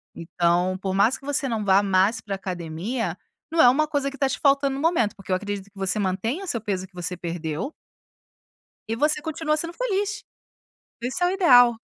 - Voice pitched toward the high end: Yes, high, 225 Hz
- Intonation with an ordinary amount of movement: No, wide, 7.4 semitones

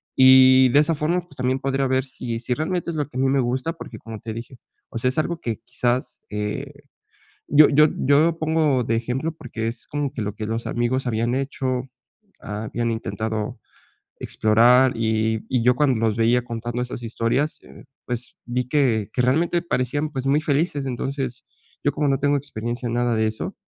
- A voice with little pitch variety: No, average, 3.6 semitones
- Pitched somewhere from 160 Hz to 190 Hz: No, low, 125 Hz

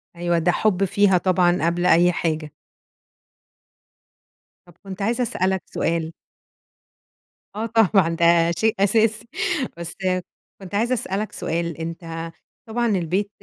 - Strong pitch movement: No, average, 3.7 semitones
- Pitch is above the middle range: No, medium, 180 Hz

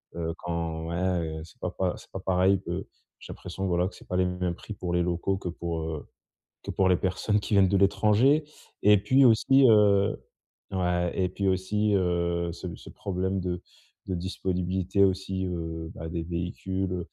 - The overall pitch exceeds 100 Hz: No, very low, 90 Hz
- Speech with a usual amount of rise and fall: No, narrow, 1.9 semitones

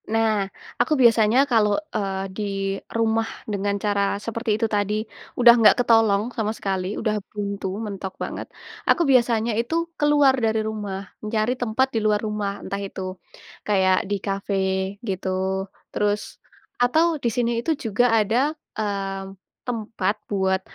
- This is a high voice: Yes, high, 215 Hz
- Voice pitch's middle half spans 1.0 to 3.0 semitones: Yes, narrow, 2.5 semitones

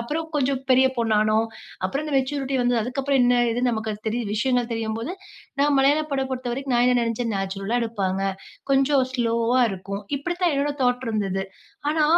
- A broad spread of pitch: No, average, 3.4 semitones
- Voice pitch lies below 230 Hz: No, high, 245 Hz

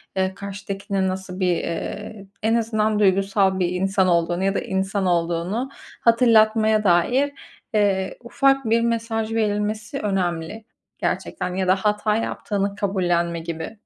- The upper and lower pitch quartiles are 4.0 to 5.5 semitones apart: No, average, 2.7 semitones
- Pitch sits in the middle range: No, high, 200 Hz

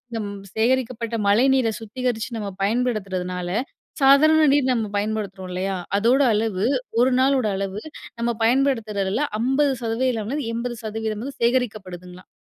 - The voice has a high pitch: Yes, high, 225 Hz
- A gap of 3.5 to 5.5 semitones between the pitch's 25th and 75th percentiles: Yes, average, 4.0 semitones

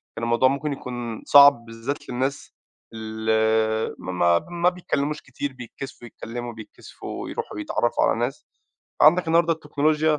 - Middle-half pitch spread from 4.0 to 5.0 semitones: Yes, average, 4.4 semitones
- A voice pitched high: No, low, 130 Hz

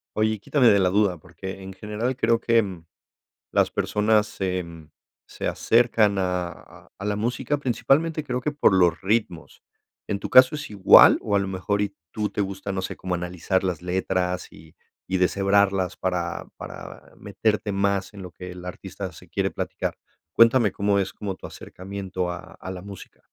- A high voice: No, low, 100 Hz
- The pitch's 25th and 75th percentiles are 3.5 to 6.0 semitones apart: No, average, 2.7 semitones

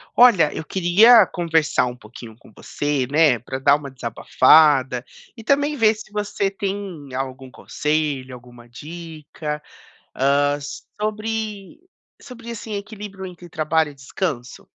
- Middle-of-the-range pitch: Yes, medium, 160 Hz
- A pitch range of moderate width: No, wide, 7.2 semitones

